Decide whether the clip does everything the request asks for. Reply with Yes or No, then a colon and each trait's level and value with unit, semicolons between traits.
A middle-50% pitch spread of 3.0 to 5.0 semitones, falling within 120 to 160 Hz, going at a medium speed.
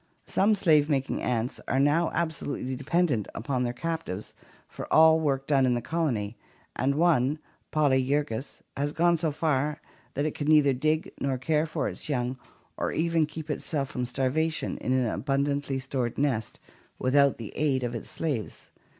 Yes: average, 3.3 semitones; medium, 140 Hz; average, 165 wpm